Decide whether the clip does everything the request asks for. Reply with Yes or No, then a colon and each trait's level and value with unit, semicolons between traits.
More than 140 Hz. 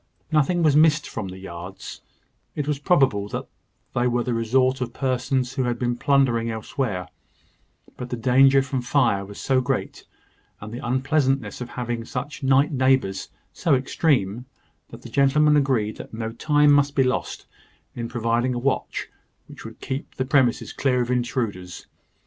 No: low, 125 Hz